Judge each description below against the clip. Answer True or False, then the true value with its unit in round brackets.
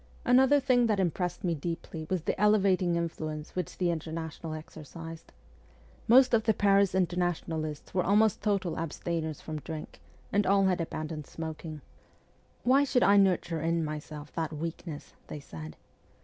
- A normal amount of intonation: True (4.0 semitones)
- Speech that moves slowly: False (160 wpm)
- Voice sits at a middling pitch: True (170 Hz)